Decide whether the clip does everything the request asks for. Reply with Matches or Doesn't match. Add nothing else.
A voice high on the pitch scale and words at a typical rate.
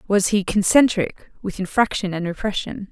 Matches